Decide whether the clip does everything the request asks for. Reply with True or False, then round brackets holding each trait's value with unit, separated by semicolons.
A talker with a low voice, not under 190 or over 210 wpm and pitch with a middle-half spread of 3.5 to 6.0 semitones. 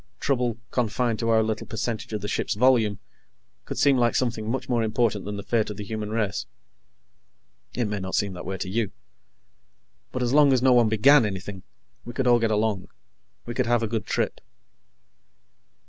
False (115 Hz; 195 wpm; 2.7 semitones)